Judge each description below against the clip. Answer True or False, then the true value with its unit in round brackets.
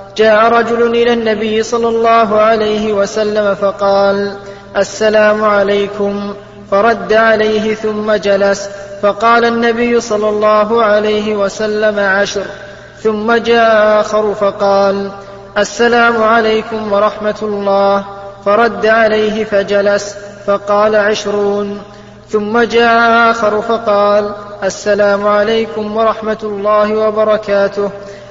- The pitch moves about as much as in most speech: False (1.4 semitones)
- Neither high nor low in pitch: False (210 Hz)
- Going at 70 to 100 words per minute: True (95 wpm)